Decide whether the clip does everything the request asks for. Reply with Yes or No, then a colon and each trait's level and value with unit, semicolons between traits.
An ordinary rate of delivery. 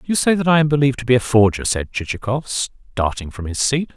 No: fast, 240 wpm